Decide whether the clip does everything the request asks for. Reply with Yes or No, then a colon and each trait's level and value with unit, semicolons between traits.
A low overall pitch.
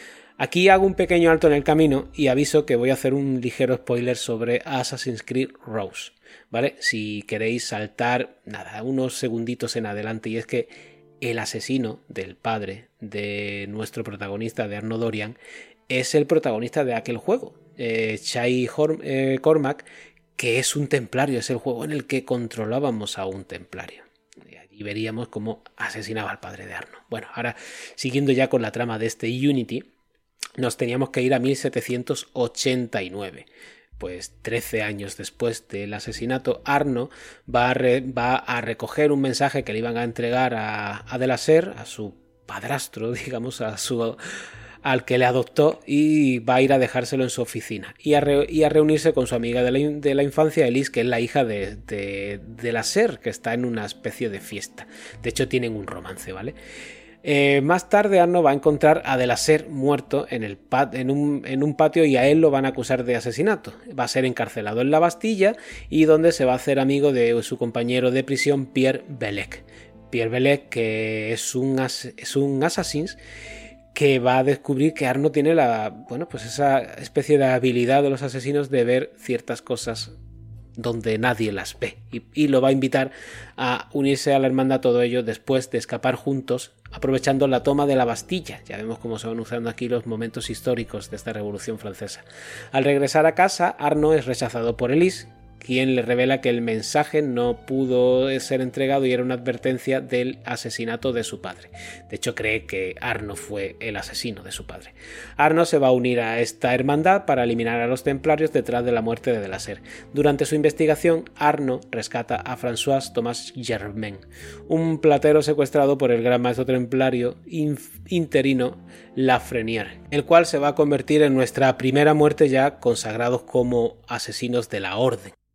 Yes: low, 125 Hz